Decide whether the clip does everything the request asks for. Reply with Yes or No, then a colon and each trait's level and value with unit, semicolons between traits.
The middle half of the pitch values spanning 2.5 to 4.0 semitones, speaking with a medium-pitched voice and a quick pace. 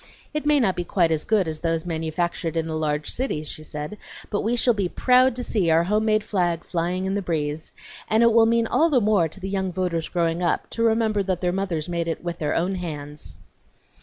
No: average, 4.7 semitones; medium, 180 Hz; fast, 235 wpm